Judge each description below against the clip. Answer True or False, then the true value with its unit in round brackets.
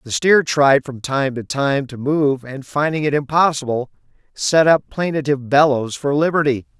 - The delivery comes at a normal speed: True (170 wpm)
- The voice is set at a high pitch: False (140 Hz)